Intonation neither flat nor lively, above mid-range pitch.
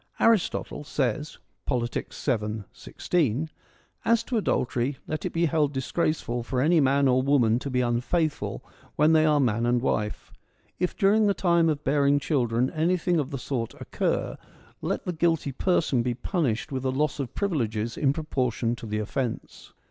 No: average, 4.7 semitones; medium, 140 Hz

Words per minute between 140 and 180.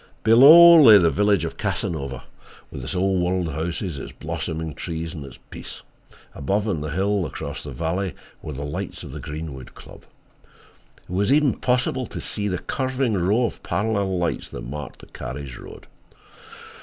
Yes: average, 170 wpm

